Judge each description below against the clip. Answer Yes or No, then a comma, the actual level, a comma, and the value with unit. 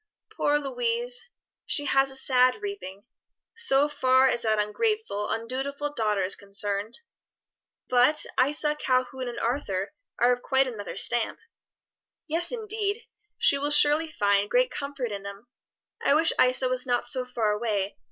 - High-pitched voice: Yes, very high, 260 Hz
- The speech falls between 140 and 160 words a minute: Yes, average, 145 wpm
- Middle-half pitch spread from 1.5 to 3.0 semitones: No, average, 5.0 semitones